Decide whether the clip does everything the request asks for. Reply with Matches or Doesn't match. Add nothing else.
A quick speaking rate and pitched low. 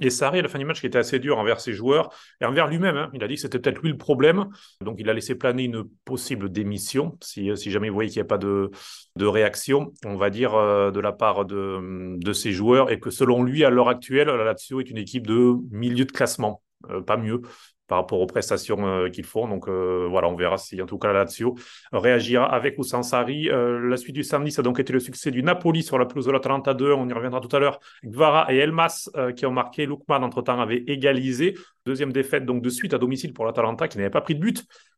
Matches